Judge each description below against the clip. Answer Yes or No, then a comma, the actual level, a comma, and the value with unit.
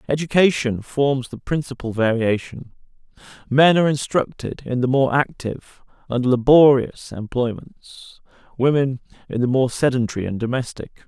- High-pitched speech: No, low, 130 Hz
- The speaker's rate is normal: No, slow, 120 wpm